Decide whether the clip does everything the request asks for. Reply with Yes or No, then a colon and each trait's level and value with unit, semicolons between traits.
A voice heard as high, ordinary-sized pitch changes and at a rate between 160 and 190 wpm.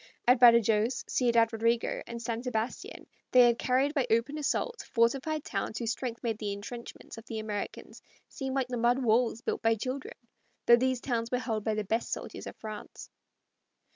No: high, 235 Hz; narrow, 2.1 semitones; average, 180 wpm